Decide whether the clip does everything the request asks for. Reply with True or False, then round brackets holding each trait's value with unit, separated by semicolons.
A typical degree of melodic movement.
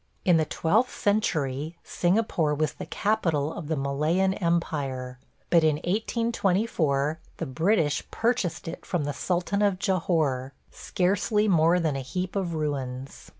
True (4.6 semitones)